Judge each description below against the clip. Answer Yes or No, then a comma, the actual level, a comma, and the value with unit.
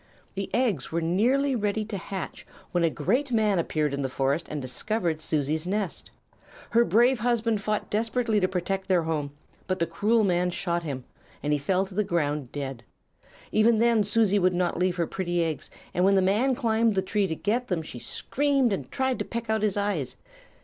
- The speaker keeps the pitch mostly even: No, average, 5.0 semitones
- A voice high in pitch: Yes, high, 195 Hz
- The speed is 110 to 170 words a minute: No, average, 200 wpm